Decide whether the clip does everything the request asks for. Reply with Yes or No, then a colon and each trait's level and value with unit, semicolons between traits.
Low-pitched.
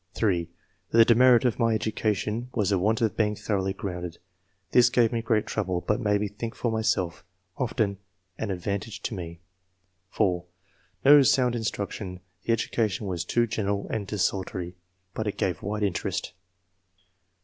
Yes: low, 105 Hz